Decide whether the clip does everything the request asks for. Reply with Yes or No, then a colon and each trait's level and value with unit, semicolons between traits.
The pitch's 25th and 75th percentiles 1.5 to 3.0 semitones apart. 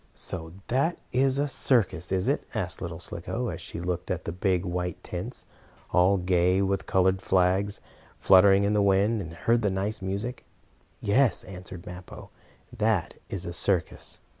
Yes: narrow, 2.5 semitones